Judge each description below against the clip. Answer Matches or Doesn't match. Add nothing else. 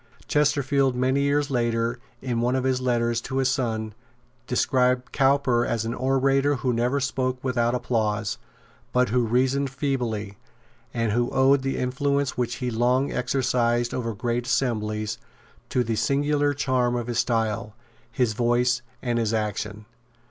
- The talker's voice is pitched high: Doesn't match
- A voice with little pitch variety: Matches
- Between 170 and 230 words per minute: Doesn't match